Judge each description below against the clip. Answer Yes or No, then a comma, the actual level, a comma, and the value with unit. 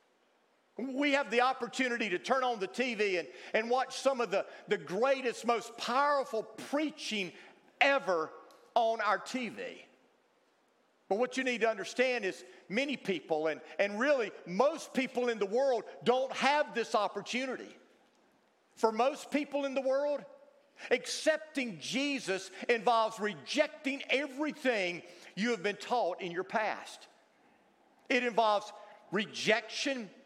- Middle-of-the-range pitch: No, high, 240 Hz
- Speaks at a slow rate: Yes, slow, 130 wpm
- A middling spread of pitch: Yes, average, 4.4 semitones